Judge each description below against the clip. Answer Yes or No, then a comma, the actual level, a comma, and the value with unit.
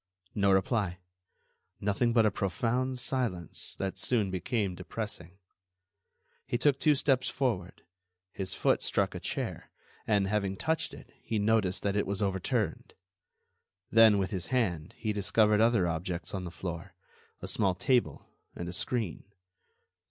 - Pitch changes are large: No, average, 3.8 semitones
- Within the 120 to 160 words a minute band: Yes, average, 140 wpm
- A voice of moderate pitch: No, low, 100 Hz